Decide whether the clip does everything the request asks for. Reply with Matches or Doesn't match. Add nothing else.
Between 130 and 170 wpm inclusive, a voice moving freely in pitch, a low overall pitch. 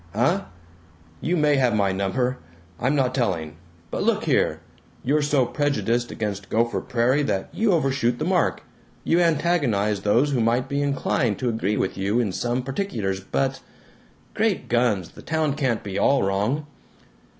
Matches